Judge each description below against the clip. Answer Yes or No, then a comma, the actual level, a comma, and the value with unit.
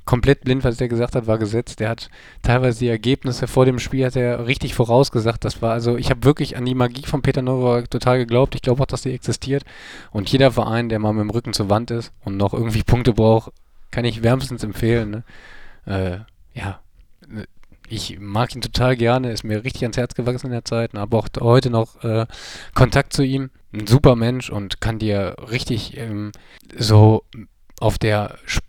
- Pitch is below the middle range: Yes, low, 120 Hz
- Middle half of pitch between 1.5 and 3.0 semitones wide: Yes, average, 2.7 semitones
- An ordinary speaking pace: No, fast, 205 wpm